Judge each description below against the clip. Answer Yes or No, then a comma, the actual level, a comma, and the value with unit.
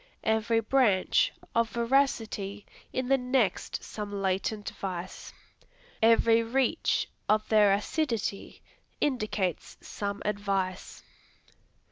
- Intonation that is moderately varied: Yes, average, 3.0 semitones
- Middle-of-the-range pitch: No, high, 215 Hz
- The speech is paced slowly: Yes, slow, 90 wpm